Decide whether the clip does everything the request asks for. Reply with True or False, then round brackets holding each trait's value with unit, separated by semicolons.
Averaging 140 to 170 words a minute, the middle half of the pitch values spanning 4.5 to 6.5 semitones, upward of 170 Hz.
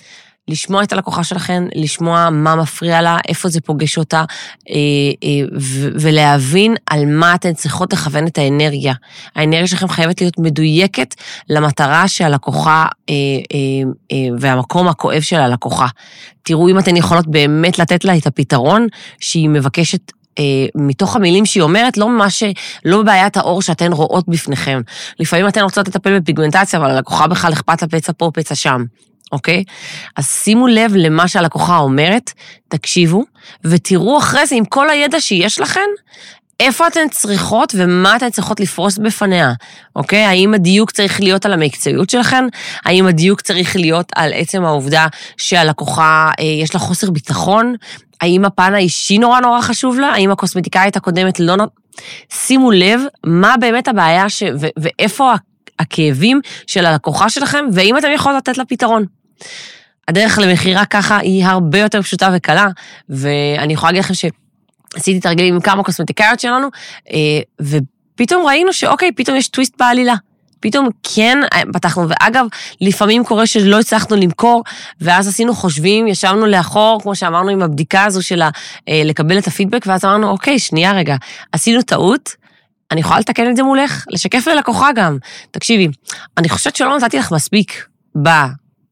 True (145 wpm; 4.9 semitones; 185 Hz)